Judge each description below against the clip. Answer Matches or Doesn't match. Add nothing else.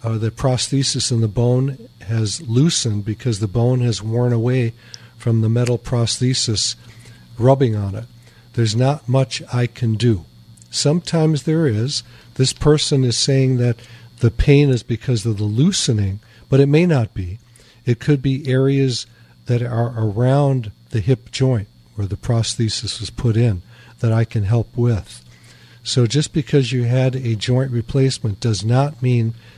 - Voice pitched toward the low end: Matches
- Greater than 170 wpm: Doesn't match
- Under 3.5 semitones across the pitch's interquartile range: Matches